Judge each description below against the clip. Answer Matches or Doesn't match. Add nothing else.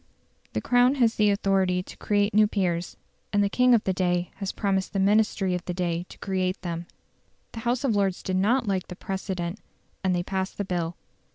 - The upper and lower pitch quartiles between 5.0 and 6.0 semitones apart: Doesn't match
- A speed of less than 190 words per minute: Doesn't match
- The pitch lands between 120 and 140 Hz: Doesn't match